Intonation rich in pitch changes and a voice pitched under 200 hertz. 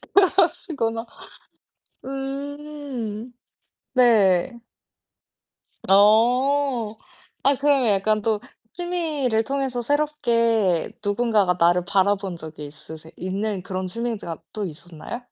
No: wide, 5.9 semitones; high, 225 Hz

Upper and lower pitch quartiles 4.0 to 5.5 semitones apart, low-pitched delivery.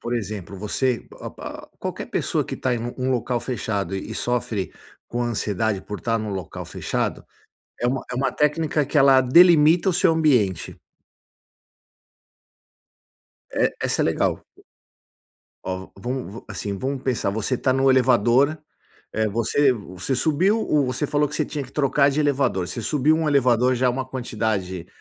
Yes: average, 4.6 semitones; low, 125 Hz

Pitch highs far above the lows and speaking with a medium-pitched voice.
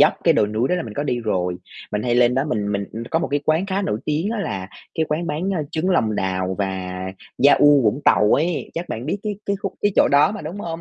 Yes: wide, 8.3 semitones; medium, 145 Hz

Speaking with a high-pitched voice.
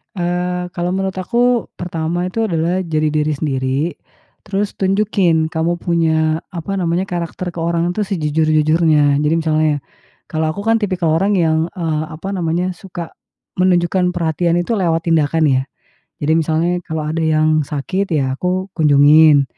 No: medium, 165 Hz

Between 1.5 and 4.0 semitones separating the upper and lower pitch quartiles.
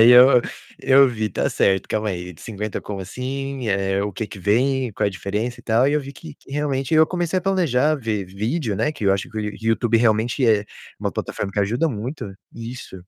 No: average, 4.9 semitones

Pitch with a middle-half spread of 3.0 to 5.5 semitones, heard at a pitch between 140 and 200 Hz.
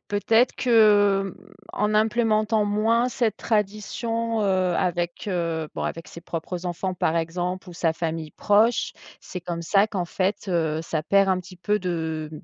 Yes: average, 3.8 semitones; high, 190 Hz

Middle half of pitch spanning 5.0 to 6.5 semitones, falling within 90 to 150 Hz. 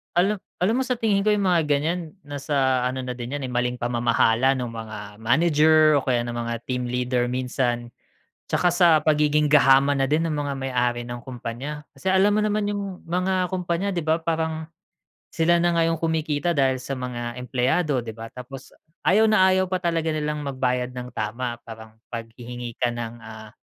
Yes: wide, 5.4 semitones; medium, 140 Hz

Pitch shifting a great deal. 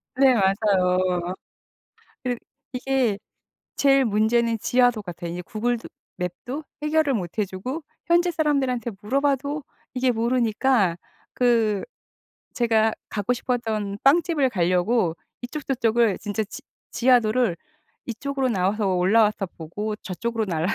No: average, 4.5 semitones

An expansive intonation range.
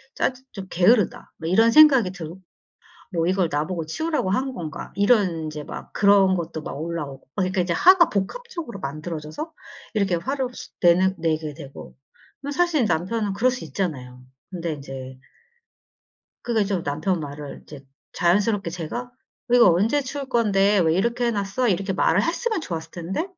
Yes: wide, 6.4 semitones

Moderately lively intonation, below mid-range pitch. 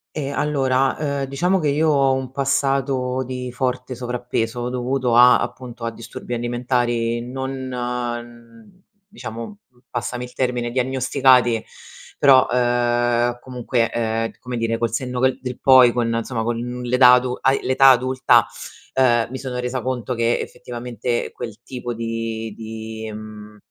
No: narrow, 1.7 semitones; low, 125 Hz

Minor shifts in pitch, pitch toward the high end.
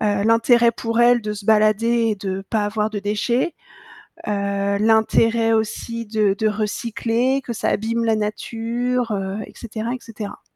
Yes: narrow, 1.8 semitones; high, 220 Hz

